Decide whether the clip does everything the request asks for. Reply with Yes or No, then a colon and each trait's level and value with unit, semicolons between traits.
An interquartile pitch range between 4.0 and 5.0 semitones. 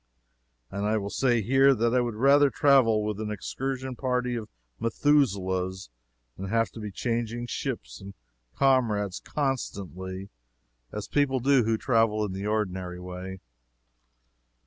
Yes: average, 4.7 semitones